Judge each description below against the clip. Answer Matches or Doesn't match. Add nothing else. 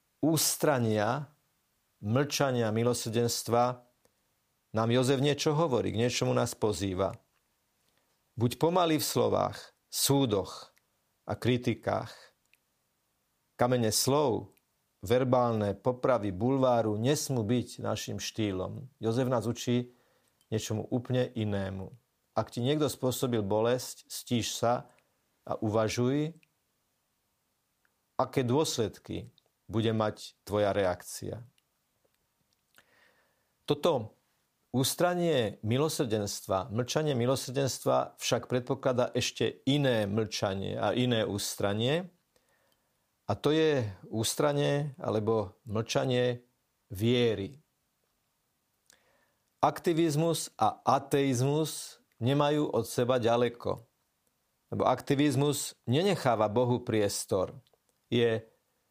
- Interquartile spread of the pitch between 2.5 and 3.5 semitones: Doesn't match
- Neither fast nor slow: Doesn't match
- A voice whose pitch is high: Doesn't match